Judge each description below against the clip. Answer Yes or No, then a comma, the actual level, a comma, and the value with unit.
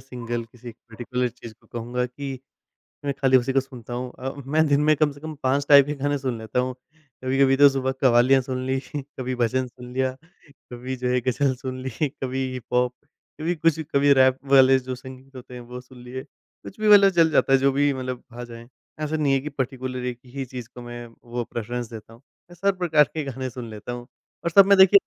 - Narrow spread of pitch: Yes, narrow, 2.1 semitones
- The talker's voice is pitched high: No, low, 130 Hz